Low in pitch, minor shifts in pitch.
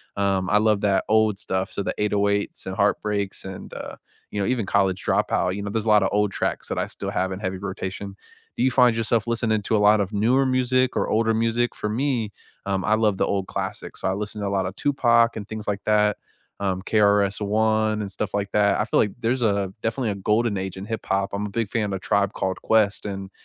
Yes: low, 105 Hz; narrow, 2.1 semitones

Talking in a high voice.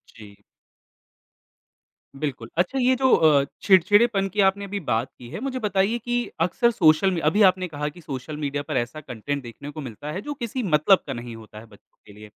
No: medium, 155 Hz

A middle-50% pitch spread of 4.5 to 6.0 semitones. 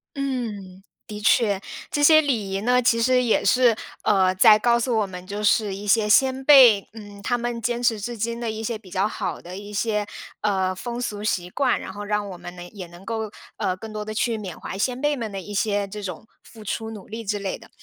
No: average, 3.1 semitones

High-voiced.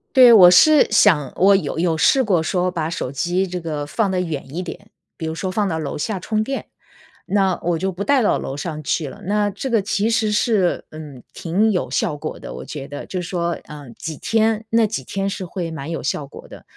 No: medium, 180 Hz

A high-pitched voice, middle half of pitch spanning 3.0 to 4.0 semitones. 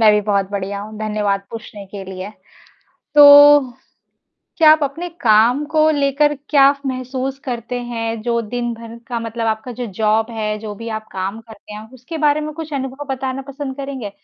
No: high, 235 Hz; average, 4.4 semitones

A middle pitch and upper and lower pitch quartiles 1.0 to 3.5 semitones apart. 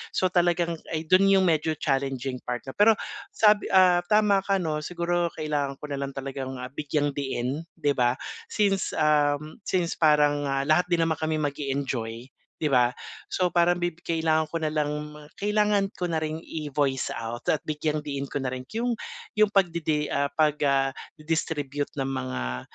No: medium, 150 Hz; average, 3.9 semitones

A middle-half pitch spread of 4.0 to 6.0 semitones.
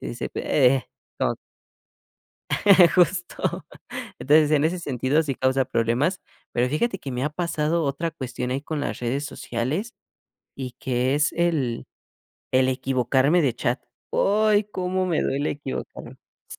Yes: average, 4.7 semitones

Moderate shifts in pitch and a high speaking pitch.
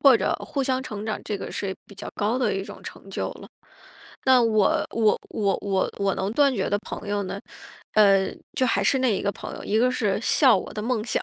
Yes: average, 3.9 semitones; high, 215 Hz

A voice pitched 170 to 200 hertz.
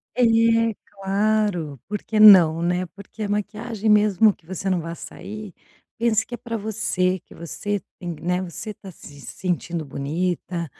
Yes: high, 190 Hz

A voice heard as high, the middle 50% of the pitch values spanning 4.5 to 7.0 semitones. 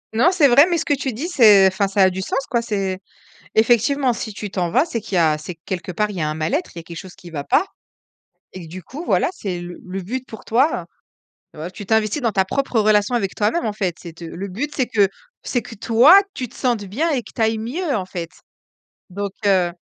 Yes: high, 210 Hz; average, 5.2 semitones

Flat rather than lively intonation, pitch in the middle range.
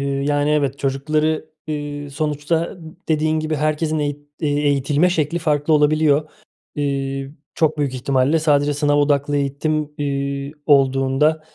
Yes: narrow, 1.7 semitones; medium, 145 Hz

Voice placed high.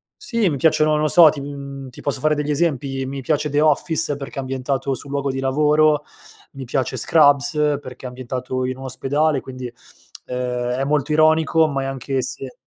No: medium, 140 Hz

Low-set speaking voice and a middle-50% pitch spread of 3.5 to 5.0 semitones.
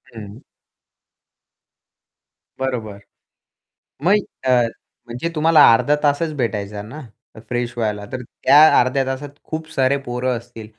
Yes: low, 125 Hz; average, 4.3 semitones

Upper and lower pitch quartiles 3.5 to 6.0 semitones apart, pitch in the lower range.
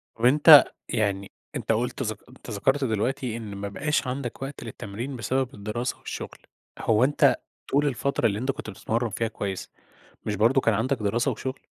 Yes: average, 4.1 semitones; low, 115 Hz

